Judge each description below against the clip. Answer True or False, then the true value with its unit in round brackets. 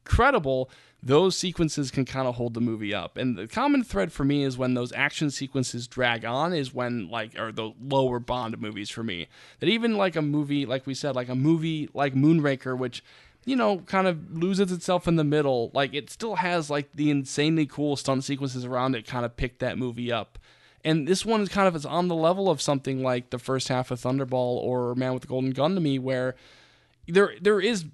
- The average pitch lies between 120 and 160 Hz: True (135 Hz)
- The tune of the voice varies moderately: True (4.4 semitones)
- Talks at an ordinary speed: False (225 wpm)